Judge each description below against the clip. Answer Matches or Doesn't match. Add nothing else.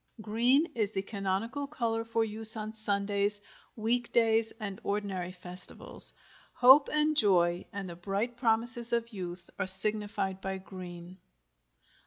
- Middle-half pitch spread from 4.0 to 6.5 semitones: Doesn't match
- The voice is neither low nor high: Doesn't match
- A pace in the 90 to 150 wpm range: Matches